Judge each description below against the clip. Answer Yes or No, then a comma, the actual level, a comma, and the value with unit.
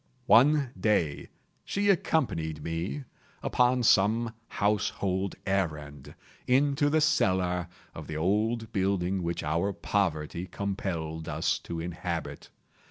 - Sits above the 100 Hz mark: No, very low, 95 Hz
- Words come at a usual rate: No, slow, 105 wpm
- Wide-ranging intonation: Yes, wide, 6.0 semitones